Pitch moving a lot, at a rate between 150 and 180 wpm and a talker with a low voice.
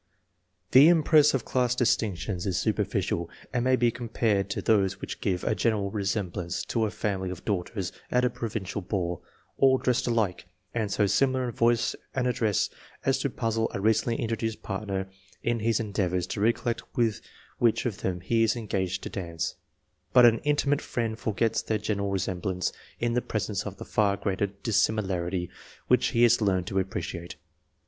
No: average, 3.5 semitones; average, 170 wpm; low, 110 Hz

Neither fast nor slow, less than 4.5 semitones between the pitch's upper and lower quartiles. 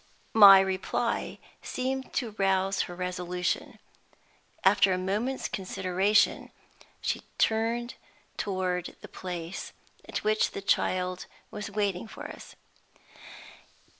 No: slow, 105 wpm; average, 2.7 semitones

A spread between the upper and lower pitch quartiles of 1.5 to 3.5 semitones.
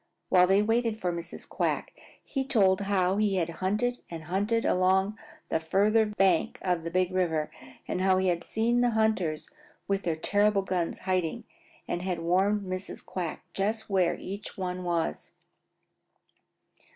Yes: average, 2.8 semitones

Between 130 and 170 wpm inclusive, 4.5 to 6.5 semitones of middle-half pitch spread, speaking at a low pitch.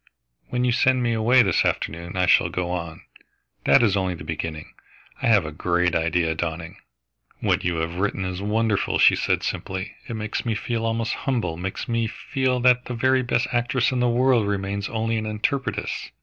No: average, 190 wpm; average, 5.2 semitones; low, 105 Hz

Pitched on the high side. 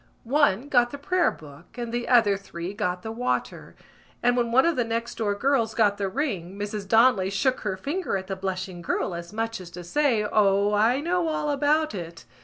Yes: high, 220 Hz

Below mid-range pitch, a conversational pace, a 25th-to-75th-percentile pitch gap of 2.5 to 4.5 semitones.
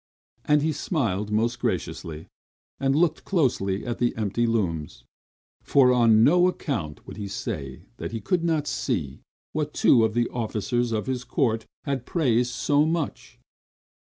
No: low, 120 Hz; average, 155 wpm; average, 5.2 semitones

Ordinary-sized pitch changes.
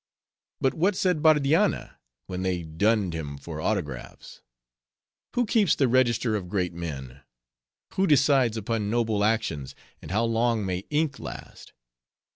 No: wide, 8.1 semitones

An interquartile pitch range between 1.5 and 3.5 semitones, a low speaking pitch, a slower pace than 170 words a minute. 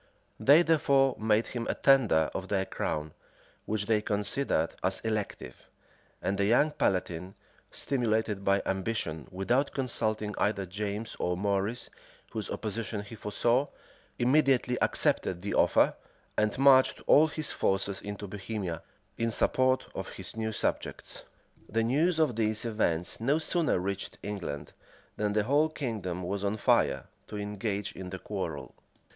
No: average, 4.0 semitones; low, 105 Hz; average, 140 wpm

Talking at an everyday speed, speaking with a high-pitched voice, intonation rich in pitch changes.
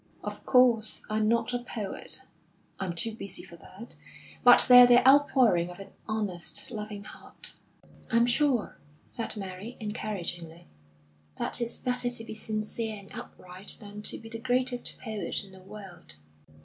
No: average, 155 wpm; high, 215 Hz; average, 3.7 semitones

